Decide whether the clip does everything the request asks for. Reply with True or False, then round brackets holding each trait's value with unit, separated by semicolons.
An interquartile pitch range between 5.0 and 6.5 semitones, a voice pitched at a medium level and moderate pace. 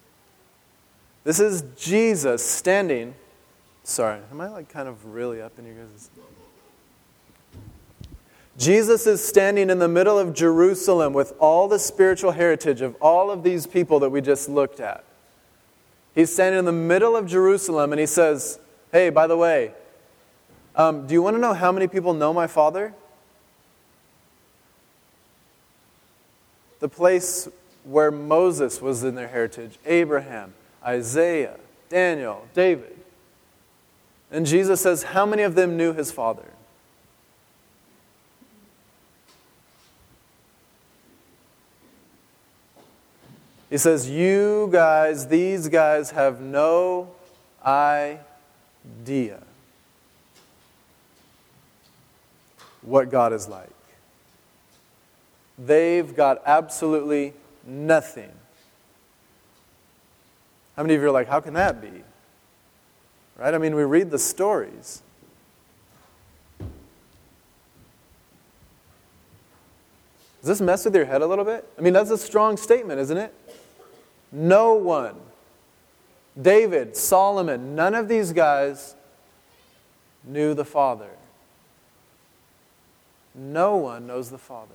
False (5.6 semitones; 155 Hz; 110 wpm)